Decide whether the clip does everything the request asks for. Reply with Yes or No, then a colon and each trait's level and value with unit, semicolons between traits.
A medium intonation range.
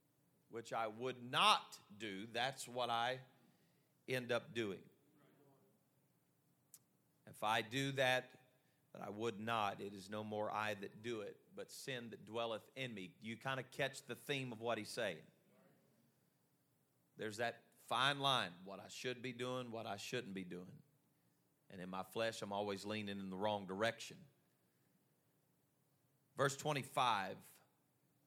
Yes: average, 4.3 semitones